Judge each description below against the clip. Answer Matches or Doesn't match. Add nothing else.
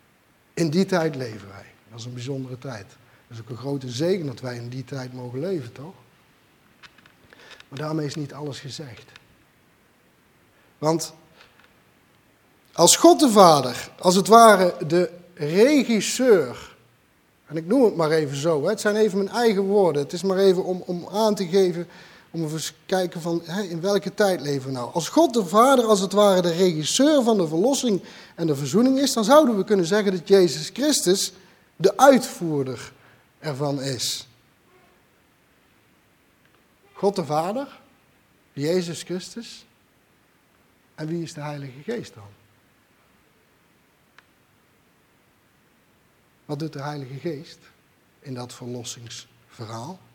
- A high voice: Doesn't match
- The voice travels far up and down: Matches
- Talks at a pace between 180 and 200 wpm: Doesn't match